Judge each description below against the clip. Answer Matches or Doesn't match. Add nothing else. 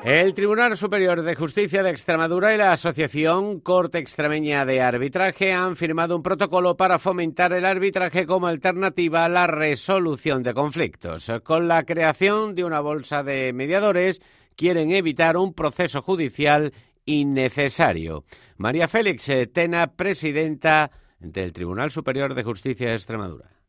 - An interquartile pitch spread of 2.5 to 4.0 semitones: Doesn't match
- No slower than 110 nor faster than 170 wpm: Matches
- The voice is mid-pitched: Matches